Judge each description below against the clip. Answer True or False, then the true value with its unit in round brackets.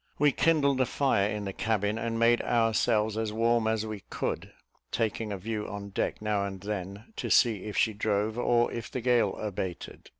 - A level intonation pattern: True (2.3 semitones)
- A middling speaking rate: True (195 wpm)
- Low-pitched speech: True (110 Hz)